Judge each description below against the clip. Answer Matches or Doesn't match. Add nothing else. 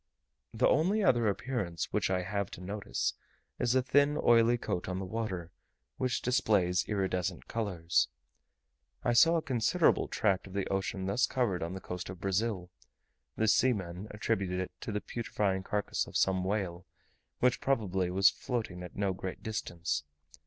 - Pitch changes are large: Doesn't match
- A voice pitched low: Matches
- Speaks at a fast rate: Doesn't match